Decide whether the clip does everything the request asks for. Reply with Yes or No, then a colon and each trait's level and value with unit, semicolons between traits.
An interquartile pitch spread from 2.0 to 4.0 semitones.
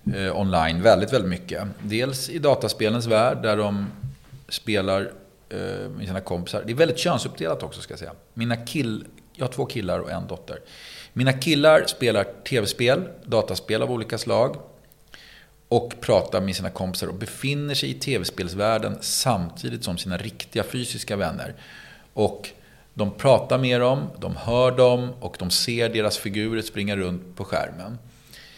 No: average, 4.6 semitones